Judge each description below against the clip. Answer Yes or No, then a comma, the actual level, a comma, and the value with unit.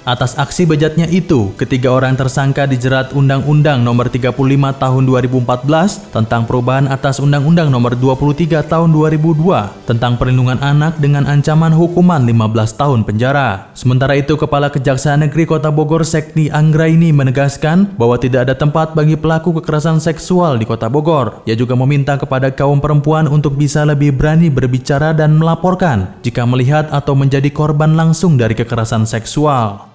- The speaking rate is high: Yes, fast, 145 wpm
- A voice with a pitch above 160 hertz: No, medium, 145 Hz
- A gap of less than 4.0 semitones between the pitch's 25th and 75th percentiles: Yes, average, 3.4 semitones